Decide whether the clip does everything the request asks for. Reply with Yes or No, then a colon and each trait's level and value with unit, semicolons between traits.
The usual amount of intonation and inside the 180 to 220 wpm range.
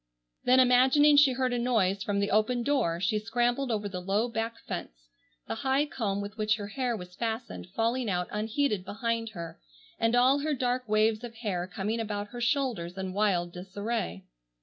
Yes: average, 3.7 semitones; average, 185 wpm